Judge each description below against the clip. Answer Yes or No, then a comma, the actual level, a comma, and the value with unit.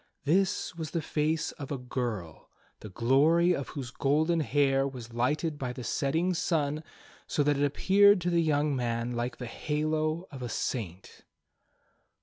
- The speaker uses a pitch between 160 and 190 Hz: No, medium, 145 Hz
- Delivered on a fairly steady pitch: No, average, 4.2 semitones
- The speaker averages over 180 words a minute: No, average, 160 wpm